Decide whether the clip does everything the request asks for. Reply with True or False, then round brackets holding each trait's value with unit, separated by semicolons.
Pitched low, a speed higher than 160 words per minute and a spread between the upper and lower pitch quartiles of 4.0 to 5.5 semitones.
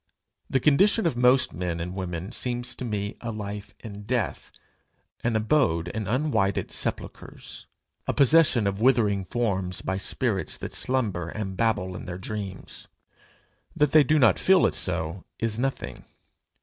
False (110 Hz; 150 wpm; 5.1 semitones)